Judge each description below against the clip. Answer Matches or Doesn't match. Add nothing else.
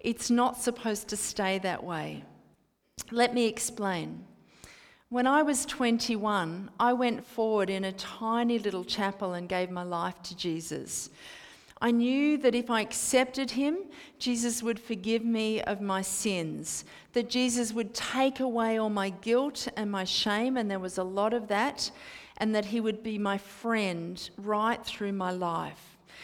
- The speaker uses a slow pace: Doesn't match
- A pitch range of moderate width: Matches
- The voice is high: Matches